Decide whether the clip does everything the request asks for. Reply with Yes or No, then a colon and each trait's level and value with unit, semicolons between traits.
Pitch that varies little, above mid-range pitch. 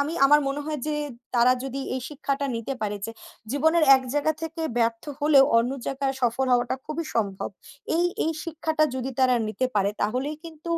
No: average, 4.1 semitones; very high, 275 Hz